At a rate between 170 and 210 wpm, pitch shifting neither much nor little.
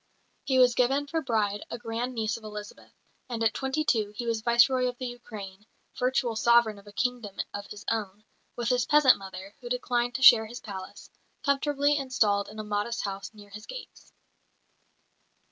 Yes: average, 180 wpm; average, 3.3 semitones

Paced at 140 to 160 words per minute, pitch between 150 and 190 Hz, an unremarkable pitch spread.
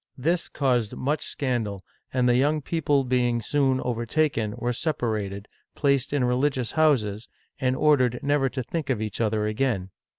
No: average, 155 wpm; low, 125 Hz; average, 3.8 semitones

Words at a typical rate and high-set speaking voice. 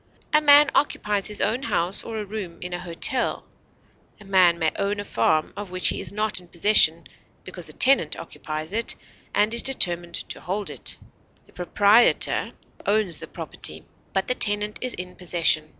Yes: average, 180 wpm; high, 200 Hz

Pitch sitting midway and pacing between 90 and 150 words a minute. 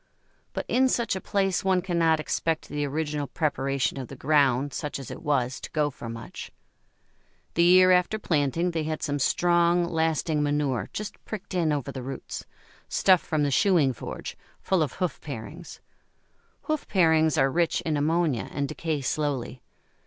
No: medium, 155 Hz; average, 165 wpm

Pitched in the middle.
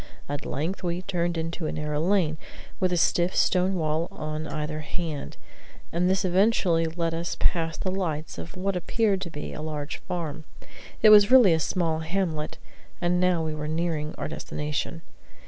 Yes: medium, 165 Hz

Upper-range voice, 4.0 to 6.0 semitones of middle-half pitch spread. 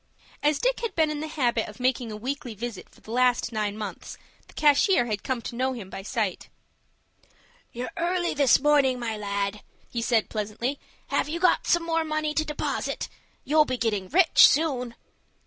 Yes: very high, 255 Hz; wide, 5.6 semitones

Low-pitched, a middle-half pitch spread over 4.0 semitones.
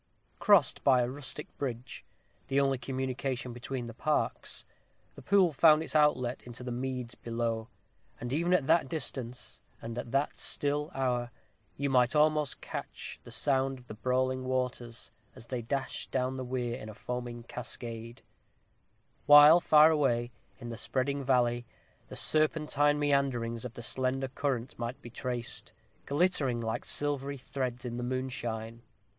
No: low, 130 Hz; average, 2.8 semitones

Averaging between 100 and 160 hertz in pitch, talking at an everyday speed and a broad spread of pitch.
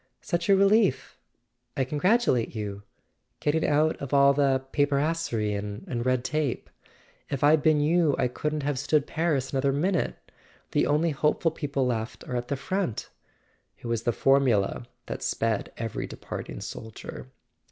No: medium, 140 Hz; average, 155 wpm; average, 4.3 semitones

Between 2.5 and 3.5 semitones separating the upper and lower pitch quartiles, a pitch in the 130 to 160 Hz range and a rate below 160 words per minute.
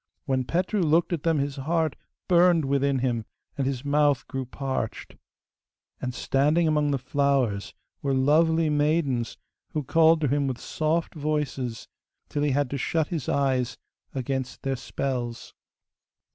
Yes: average, 2.9 semitones; medium, 140 Hz; average, 145 wpm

